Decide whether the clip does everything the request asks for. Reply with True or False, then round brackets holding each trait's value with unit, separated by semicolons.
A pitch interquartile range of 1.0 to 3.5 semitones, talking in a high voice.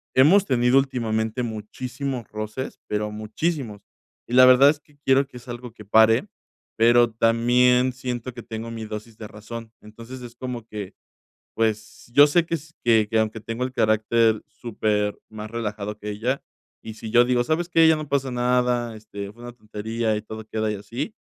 False (2.7 semitones; 115 Hz)